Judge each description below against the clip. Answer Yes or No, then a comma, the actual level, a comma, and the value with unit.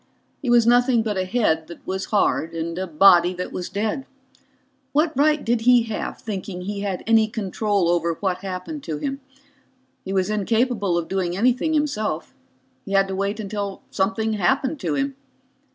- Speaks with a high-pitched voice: Yes, high, 205 Hz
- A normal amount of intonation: Yes, average, 4.6 semitones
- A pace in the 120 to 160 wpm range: No, average, 175 wpm